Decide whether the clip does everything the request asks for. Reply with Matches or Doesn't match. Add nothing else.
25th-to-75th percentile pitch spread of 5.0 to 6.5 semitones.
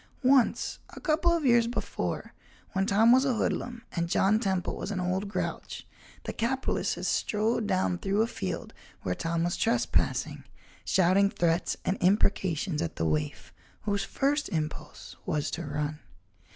Matches